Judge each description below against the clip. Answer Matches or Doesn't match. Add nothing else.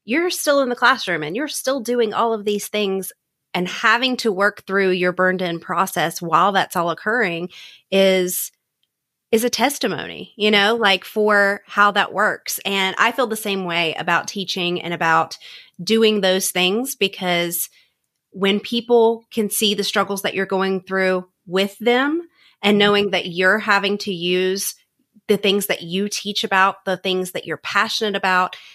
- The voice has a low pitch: Doesn't match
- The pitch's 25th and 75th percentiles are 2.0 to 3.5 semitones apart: Matches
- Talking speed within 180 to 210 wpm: Doesn't match